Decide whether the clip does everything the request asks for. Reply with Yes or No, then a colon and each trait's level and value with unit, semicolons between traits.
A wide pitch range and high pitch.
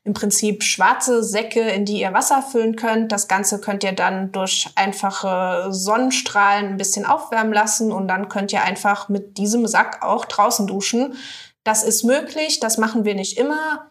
No: average, 2.7 semitones; high, 210 Hz